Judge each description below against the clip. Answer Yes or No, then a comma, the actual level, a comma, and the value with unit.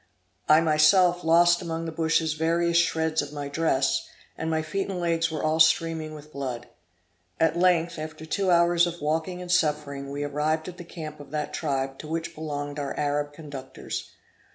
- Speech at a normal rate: Yes, average, 185 wpm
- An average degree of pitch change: No, narrow, 2.3 semitones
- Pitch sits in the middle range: Yes, medium, 160 Hz